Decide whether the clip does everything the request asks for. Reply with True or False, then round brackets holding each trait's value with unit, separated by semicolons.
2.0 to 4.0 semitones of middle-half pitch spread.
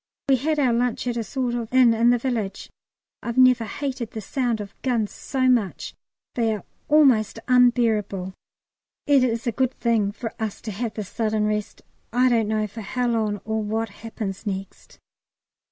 True (2.7 semitones)